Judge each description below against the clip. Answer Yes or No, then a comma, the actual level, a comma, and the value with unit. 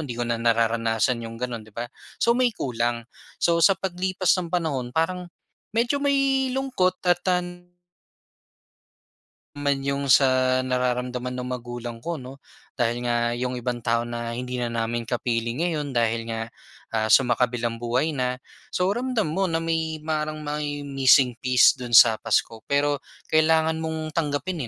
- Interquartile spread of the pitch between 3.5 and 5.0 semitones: No, wide, 5.4 semitones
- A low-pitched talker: Yes, low, 130 Hz